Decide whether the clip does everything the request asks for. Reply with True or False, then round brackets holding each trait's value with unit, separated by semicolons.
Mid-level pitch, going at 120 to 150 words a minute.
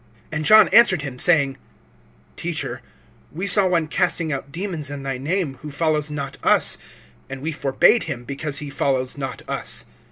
False (150 Hz; 165 wpm)